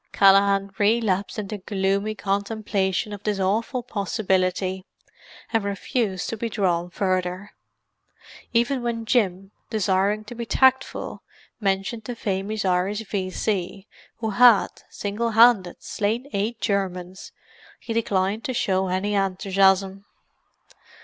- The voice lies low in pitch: No, high, 200 Hz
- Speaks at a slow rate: Yes, slow, 115 wpm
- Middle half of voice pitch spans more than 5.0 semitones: No, narrow, 2.6 semitones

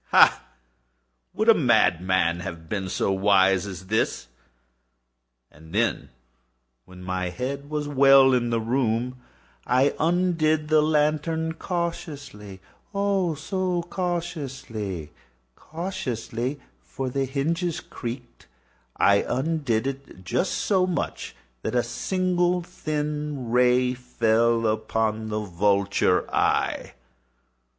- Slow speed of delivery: Yes, slow, 95 wpm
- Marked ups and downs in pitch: Yes, wide, 7.7 semitones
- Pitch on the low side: Yes, low, 125 Hz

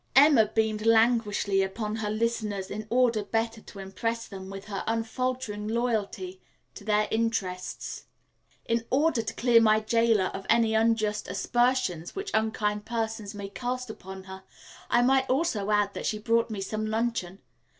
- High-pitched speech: Yes, high, 220 Hz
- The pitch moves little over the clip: Yes, narrow, 2.2 semitones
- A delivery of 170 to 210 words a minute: No, average, 160 wpm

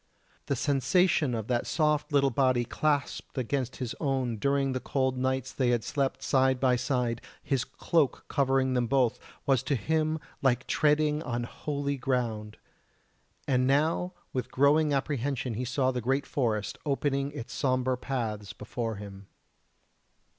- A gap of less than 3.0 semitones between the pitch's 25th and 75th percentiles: Yes, narrow, 2.6 semitones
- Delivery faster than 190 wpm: No, average, 145 wpm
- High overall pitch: No, low, 130 Hz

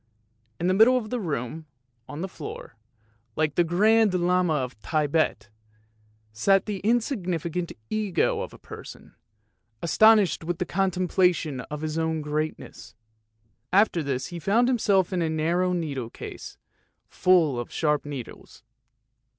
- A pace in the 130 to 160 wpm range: Yes, average, 140 wpm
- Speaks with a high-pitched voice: No, medium, 175 Hz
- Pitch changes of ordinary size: Yes, average, 4.0 semitones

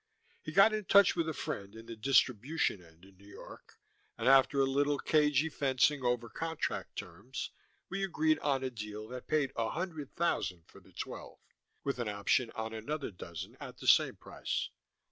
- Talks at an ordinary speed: Yes, average, 185 wpm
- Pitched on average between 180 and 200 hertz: No, low, 135 Hz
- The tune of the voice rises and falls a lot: Yes, wide, 5.8 semitones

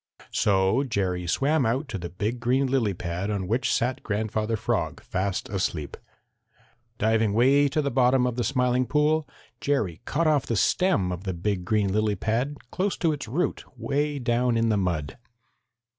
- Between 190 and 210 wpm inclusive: No, average, 175 wpm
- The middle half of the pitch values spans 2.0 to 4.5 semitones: No, wide, 5.4 semitones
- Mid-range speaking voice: No, low, 115 Hz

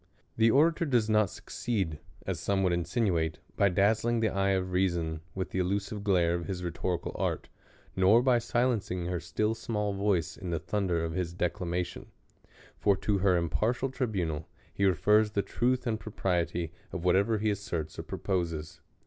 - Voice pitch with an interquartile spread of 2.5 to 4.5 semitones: Yes, average, 3.8 semitones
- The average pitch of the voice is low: Yes, very low, 95 Hz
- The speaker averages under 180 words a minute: Yes, average, 170 wpm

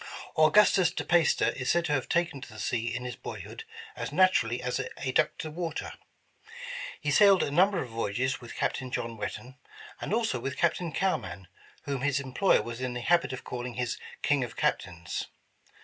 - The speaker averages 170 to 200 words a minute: Yes, average, 185 wpm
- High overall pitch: No, low, 135 Hz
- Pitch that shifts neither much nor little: No, wide, 5.8 semitones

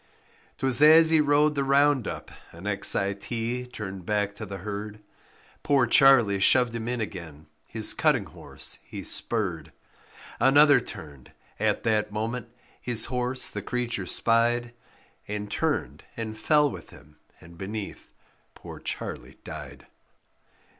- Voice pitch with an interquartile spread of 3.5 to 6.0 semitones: Yes, average, 4.2 semitones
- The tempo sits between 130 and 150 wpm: Yes, average, 140 wpm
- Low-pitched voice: Yes, low, 115 Hz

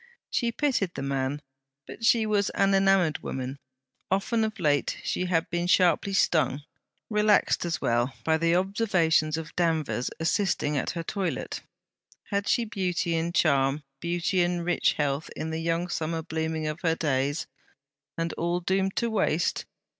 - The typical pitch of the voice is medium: Yes, medium, 170 Hz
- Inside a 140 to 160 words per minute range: Yes, average, 155 wpm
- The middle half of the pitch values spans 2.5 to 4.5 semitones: Yes, average, 3.7 semitones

